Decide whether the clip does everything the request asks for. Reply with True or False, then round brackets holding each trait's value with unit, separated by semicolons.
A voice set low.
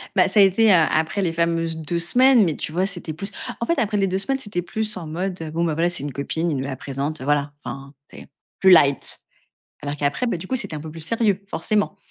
False (170 Hz)